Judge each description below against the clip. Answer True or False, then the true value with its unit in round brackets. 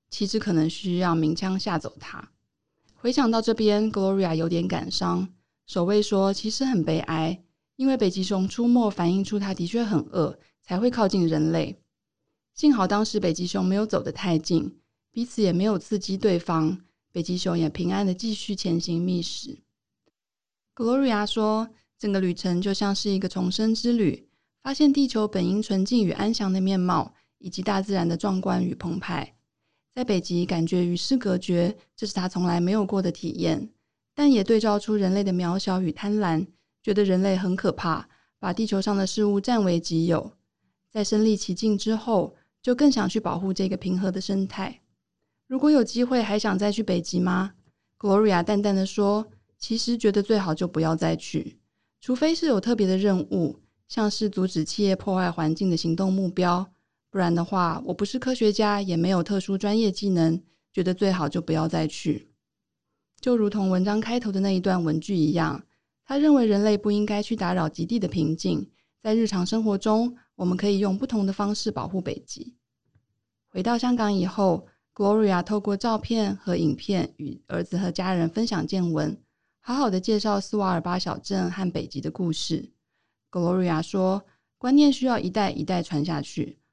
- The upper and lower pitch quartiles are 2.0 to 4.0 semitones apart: True (3.4 semitones)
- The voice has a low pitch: False (190 Hz)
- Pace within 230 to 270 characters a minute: False (280 characters per minute)